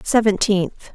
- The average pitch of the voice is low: No, high, 200 Hz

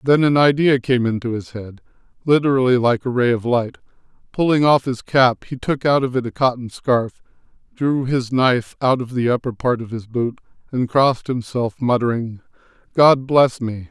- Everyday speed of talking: Yes, average, 185 wpm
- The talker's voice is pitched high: No, low, 125 Hz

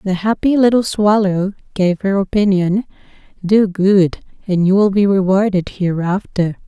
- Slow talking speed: Yes, slow, 125 wpm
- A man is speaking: No, female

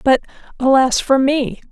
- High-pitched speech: Yes, very high, 265 Hz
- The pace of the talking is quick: No, average, 140 wpm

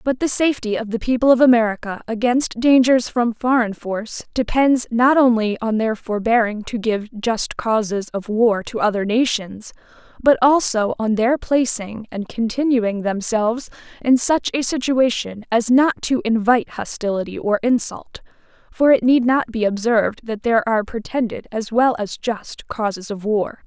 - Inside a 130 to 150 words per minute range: No, average, 160 wpm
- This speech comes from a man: No, female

